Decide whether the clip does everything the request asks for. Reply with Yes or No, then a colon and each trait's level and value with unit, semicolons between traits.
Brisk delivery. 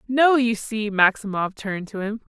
No: average, 180 wpm